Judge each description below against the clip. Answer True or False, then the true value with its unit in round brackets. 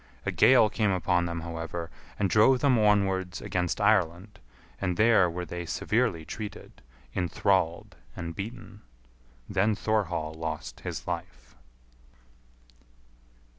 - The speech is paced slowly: True (115 wpm)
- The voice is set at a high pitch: False (95 Hz)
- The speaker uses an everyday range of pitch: True (4.0 semitones)